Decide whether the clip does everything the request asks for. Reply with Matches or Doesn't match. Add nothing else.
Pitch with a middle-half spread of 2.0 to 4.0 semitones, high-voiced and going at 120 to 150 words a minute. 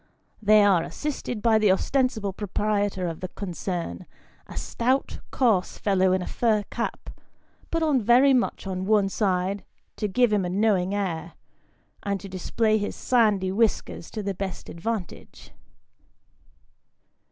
Matches